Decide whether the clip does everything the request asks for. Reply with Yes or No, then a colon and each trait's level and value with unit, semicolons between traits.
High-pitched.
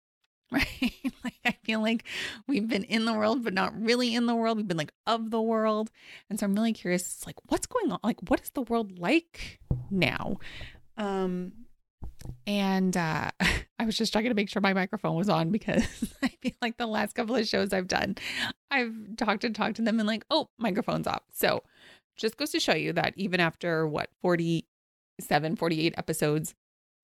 Yes: high, 220 Hz